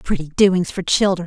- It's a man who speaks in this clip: No, female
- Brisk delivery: No, average, 190 wpm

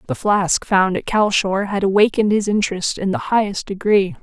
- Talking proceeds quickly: No, average, 185 wpm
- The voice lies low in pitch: No, high, 200 Hz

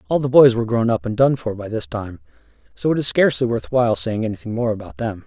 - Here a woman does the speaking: No, male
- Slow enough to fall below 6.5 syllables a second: No, 6.6 syllables/s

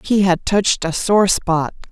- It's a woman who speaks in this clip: Yes, female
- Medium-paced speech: Yes, average, 190 wpm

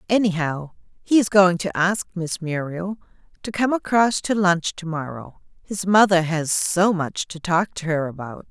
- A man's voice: No, female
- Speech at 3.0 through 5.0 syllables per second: Yes, 4.4 syllables/s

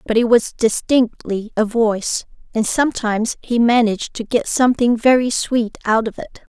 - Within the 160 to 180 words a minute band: Yes, average, 165 wpm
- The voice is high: Yes, high, 230 Hz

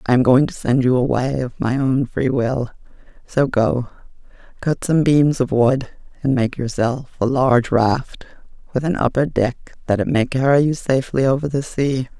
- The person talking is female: Yes, female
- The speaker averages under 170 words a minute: No, average, 185 wpm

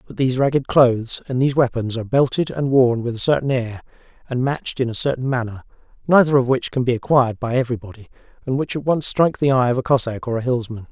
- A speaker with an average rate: No, fast, 230 wpm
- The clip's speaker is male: Yes, male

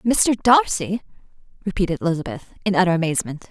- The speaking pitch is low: No, medium, 185 Hz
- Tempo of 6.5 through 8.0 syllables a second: Yes, 6.6 syllables/s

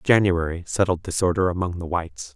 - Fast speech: No, average, 155 wpm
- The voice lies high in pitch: No, very low, 90 Hz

